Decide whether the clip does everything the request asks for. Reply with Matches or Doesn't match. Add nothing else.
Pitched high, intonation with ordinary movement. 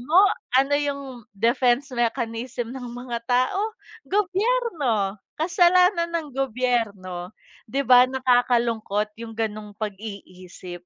Matches